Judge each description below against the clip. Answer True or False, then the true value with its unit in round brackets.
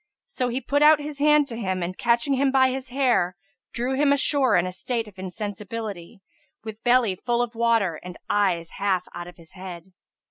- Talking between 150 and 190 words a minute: False (200 wpm)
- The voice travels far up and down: True (5.9 semitones)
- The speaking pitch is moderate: False (230 Hz)